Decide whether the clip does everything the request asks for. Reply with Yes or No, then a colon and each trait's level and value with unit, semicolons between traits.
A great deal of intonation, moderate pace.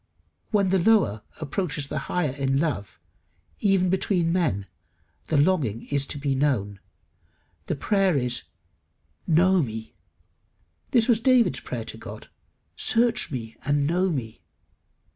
No: wide, 6.1 semitones; slow, 130 wpm